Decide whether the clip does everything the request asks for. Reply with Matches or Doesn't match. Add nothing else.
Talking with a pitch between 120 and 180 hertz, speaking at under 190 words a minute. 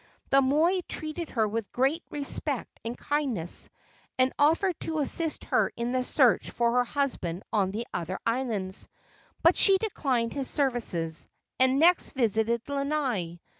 Doesn't match